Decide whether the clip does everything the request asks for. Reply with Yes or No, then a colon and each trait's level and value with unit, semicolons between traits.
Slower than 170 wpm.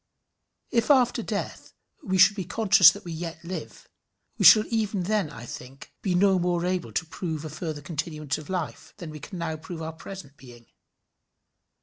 No: average, 185 wpm